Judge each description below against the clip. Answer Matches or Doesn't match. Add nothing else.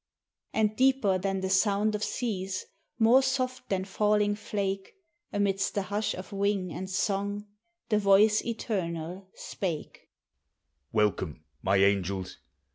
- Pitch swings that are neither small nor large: Doesn't match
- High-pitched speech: Matches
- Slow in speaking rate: Matches